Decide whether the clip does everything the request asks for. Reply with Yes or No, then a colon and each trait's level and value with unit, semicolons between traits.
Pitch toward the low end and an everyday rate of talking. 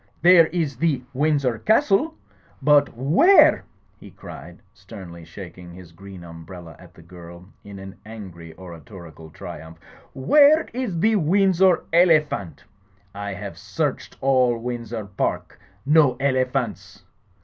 No: low, 115 Hz; slow, 125 wpm